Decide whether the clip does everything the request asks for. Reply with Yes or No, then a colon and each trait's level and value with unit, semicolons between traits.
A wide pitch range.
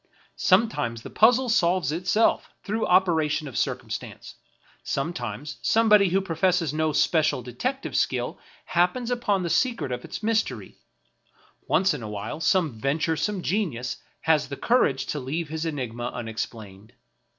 Yes: wide, 7.1 semitones